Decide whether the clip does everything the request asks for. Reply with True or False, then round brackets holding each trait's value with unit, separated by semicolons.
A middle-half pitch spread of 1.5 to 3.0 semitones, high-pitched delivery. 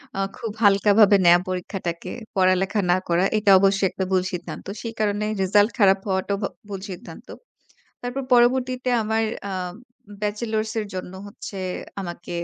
True (2.7 semitones; 200 Hz)